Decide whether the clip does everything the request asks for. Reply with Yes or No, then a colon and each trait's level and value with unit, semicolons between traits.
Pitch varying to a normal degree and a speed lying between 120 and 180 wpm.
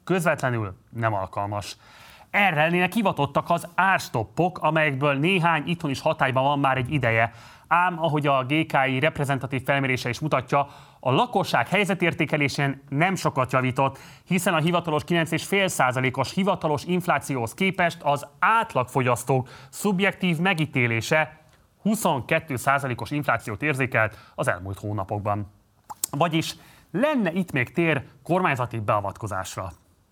No: average, 4.9 semitones; average, 110 wpm